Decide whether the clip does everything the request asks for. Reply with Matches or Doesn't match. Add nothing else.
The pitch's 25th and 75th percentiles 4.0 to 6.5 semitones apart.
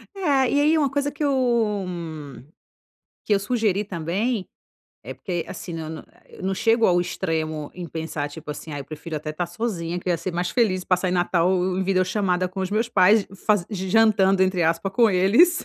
Matches